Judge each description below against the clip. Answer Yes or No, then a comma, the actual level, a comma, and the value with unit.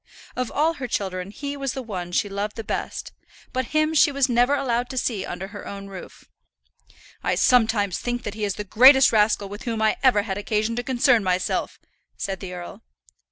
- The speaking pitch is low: No, high, 220 Hz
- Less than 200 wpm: No, fast, 205 wpm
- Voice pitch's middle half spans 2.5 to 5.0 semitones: Yes, average, 4.2 semitones